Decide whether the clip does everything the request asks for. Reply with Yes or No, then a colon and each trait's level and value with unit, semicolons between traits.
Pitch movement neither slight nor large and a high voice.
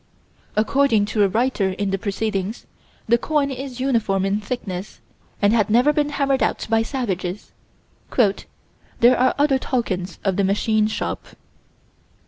Yes: average, 4.6 semitones; high, 220 Hz